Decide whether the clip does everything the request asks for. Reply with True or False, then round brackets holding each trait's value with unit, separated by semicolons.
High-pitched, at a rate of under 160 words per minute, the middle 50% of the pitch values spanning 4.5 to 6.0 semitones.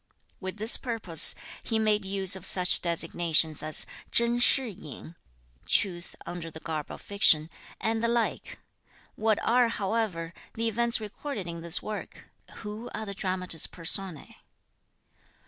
True (195 Hz; 140 wpm; 4.8 semitones)